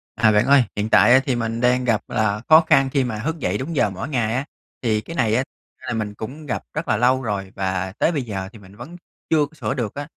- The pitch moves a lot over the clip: No, average, 4.4 semitones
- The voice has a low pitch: Yes, low, 120 Hz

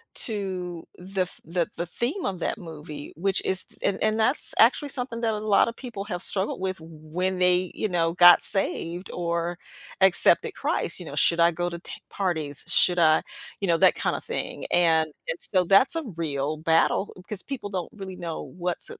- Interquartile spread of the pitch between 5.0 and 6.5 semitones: No, average, 2.8 semitones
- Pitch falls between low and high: Yes, medium, 180 Hz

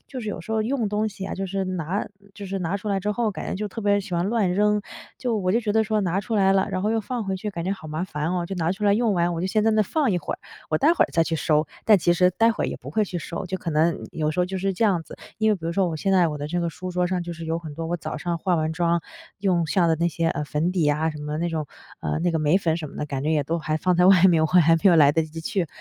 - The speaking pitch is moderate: Yes, medium, 180 Hz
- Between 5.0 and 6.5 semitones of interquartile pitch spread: No, average, 3.7 semitones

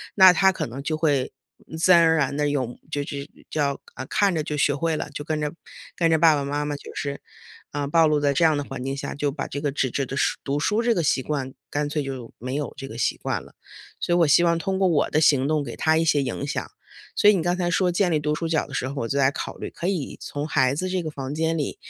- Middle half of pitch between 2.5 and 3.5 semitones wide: Yes, average, 2.8 semitones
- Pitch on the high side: No, medium, 150 Hz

